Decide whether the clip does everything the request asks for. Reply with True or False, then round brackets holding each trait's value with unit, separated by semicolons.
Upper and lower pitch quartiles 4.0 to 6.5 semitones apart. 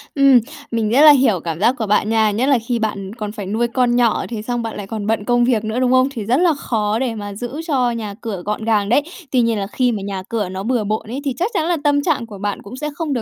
False (3.6 semitones)